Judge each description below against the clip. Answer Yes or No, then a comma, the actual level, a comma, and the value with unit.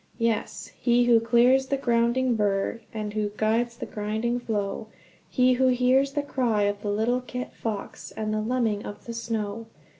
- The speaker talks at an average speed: Yes, average, 160 wpm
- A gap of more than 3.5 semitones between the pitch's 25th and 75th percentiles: No, average, 2.7 semitones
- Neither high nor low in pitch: No, high, 230 Hz